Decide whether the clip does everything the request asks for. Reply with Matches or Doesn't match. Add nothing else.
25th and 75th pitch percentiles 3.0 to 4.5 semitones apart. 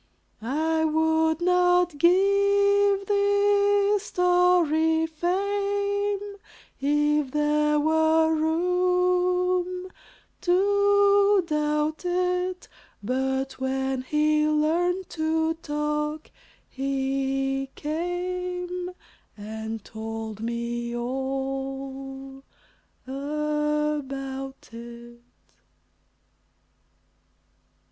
Doesn't match